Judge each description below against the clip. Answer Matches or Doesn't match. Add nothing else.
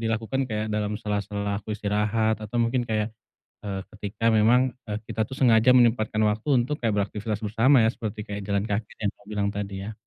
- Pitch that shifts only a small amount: Matches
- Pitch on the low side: Matches